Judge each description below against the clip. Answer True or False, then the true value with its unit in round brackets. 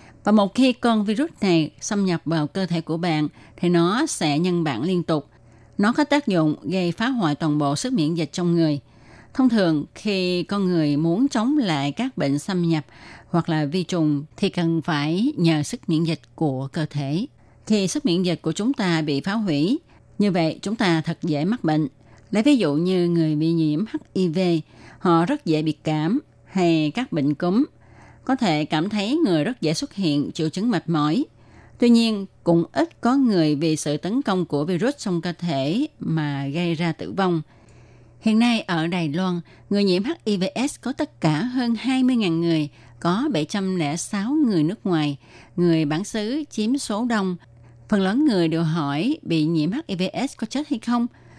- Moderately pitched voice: True (170 Hz)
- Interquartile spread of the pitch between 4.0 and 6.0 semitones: True (5.6 semitones)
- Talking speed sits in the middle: True (195 wpm)